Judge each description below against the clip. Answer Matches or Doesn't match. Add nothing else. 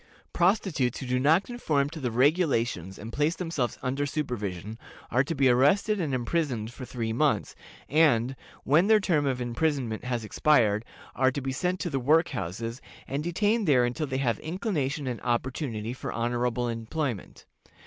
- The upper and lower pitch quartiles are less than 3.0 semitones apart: Doesn't match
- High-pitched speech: Doesn't match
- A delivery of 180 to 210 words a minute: Doesn't match